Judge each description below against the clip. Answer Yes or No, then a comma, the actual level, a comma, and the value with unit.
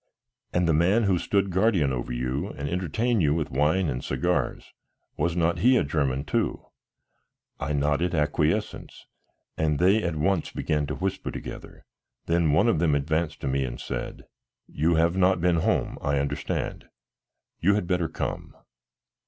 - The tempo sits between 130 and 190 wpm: Yes, average, 160 wpm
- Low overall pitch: Yes, very low, 80 Hz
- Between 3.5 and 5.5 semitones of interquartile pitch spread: Yes, average, 3.8 semitones